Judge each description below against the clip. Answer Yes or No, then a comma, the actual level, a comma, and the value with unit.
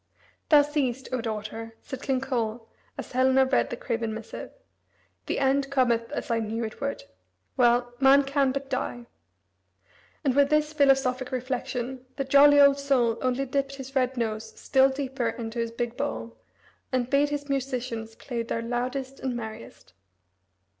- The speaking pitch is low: No, very high, 255 Hz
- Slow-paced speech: No, average, 160 wpm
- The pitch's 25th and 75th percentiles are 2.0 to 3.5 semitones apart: Yes, average, 2.8 semitones